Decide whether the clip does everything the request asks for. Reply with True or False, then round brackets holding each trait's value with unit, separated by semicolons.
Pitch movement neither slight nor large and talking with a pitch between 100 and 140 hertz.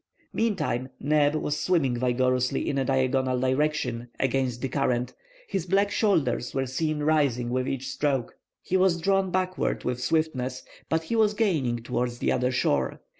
True (4.4 semitones; 135 Hz)